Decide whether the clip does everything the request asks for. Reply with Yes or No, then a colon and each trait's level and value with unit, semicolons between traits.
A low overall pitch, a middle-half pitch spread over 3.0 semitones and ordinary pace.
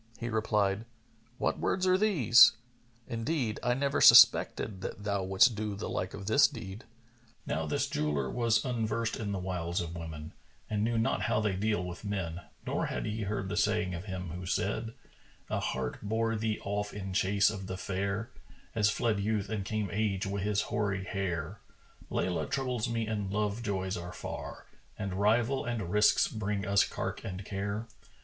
No: low, 105 Hz; average, 2.7 semitones; average, 185 wpm